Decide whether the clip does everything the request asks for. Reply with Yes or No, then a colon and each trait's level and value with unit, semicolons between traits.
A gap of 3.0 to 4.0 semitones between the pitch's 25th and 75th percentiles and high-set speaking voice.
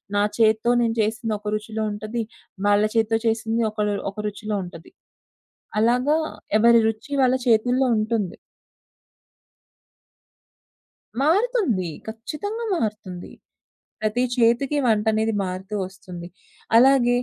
No: narrow, 2.4 semitones; high, 220 Hz